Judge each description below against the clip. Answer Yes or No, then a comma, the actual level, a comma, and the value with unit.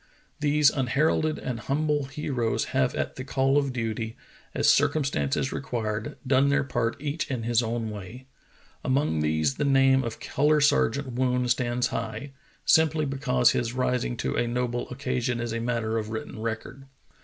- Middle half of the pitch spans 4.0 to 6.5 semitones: No, average, 3.3 semitones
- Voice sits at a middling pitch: No, low, 125 Hz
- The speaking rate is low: No, average, 160 wpm